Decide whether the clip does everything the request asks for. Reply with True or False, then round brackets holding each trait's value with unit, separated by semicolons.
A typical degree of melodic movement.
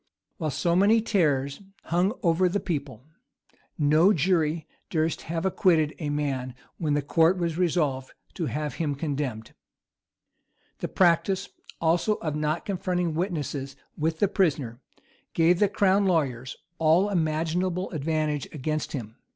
True (3.5 semitones)